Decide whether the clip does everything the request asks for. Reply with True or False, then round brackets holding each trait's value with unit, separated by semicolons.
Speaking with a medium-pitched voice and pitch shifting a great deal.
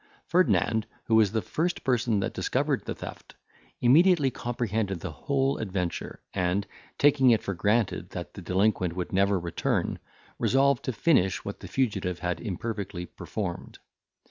False (110 Hz; 5.8 semitones)